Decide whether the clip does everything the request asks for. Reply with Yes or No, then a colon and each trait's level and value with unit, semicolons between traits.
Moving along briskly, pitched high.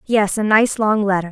Yes: fast, 230 wpm; high, 205 Hz